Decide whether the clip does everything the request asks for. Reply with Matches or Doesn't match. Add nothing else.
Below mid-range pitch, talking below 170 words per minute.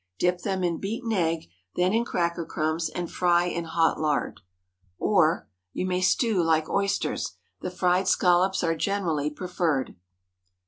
Doesn't match